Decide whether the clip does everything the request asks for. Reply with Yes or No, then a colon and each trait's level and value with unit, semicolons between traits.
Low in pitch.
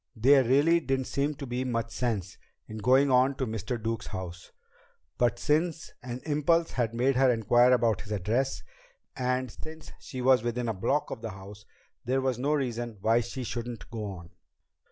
Yes: low, 125 Hz